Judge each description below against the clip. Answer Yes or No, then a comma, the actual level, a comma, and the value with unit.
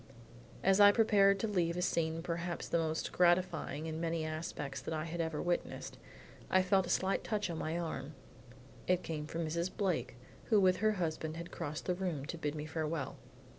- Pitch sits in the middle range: Yes, medium, 170 Hz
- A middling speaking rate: Yes, average, 195 wpm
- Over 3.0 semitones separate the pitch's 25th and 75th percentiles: No, average, 2.7 semitones